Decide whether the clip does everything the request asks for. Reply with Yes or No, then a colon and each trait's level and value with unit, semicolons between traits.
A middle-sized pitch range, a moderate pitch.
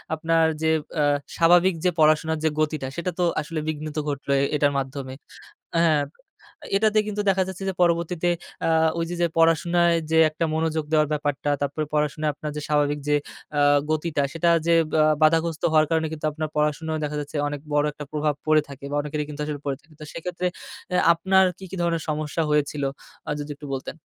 No: narrow, 2.1 semitones; medium, 155 Hz